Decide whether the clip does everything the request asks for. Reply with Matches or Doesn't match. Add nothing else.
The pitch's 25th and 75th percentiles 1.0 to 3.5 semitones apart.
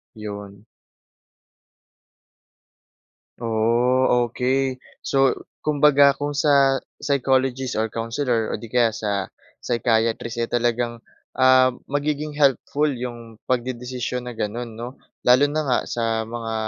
Matches